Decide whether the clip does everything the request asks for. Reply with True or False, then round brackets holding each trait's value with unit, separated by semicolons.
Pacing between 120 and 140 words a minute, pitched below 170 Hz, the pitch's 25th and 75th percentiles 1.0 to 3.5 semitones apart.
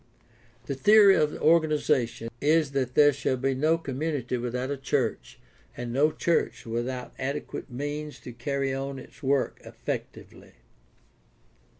True (135 wpm; 135 Hz; 2.9 semitones)